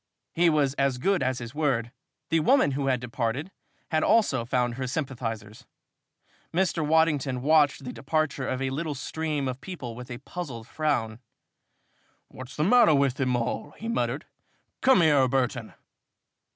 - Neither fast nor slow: Yes, average, 155 wpm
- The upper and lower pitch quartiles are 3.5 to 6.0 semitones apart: Yes, average, 4.1 semitones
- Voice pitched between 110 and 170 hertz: Yes, low, 135 Hz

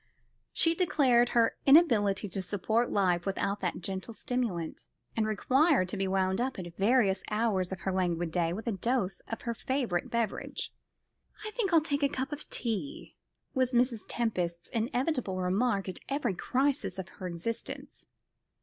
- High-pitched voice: Yes, high, 225 Hz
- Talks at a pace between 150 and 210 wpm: Yes, average, 160 wpm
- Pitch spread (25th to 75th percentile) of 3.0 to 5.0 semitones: No, wide, 5.4 semitones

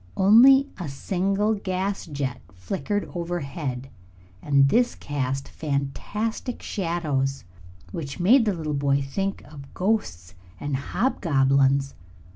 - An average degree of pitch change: No, wide, 6.3 semitones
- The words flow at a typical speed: No, slow, 105 wpm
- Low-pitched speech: No, medium, 150 Hz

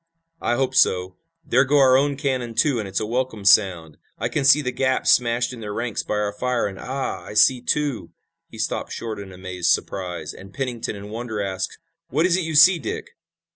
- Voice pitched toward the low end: Yes, low, 120 Hz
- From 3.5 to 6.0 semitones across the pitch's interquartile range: Yes, average, 4.7 semitones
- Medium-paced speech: No, fast, 215 wpm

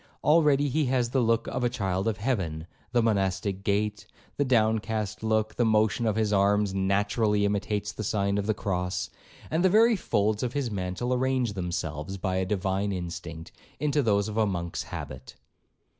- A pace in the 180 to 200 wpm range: No, average, 170 wpm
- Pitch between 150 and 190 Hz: No, low, 105 Hz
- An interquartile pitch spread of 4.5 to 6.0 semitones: No, average, 3.5 semitones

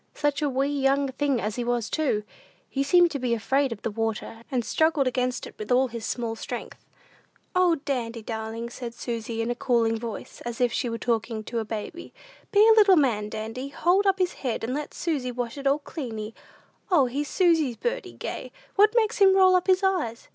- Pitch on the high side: Yes, very high, 255 Hz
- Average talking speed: No, fast, 210 wpm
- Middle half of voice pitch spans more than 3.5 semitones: Yes, wide, 5.5 semitones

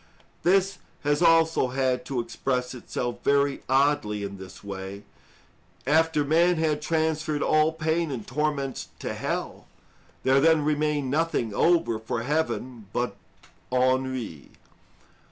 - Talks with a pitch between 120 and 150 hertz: Yes, medium, 140 Hz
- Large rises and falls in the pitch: No, average, 4.2 semitones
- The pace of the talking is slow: Yes, slow, 120 wpm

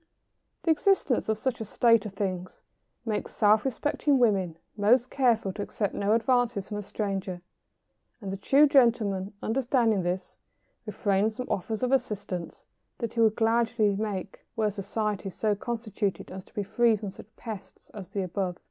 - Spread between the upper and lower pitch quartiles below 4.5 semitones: Yes, average, 3.2 semitones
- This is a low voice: No, high, 215 Hz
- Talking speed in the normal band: Yes, average, 165 wpm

